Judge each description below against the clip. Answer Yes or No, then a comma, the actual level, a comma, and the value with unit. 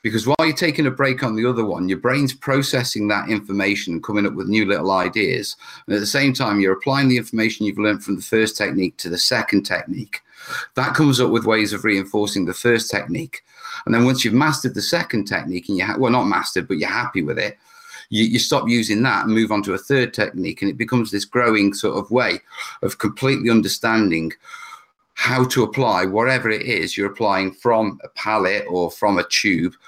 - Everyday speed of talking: No, fast, 215 wpm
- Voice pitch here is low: Yes, low, 110 Hz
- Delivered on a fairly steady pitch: No, average, 3.8 semitones